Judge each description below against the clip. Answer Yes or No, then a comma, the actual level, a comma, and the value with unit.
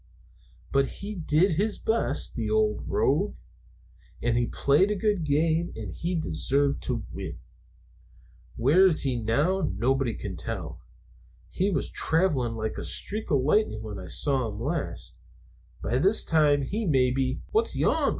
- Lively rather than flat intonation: Yes, wide, 7.2 semitones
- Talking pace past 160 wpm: No, average, 155 wpm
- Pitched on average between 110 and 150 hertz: Yes, medium, 140 Hz